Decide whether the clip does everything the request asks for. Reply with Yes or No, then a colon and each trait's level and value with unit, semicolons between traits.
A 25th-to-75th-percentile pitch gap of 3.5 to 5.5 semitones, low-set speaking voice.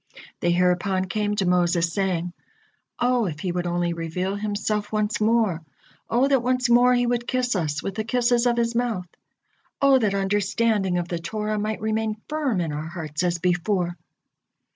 No: average, 4.8 semitones; high, 205 Hz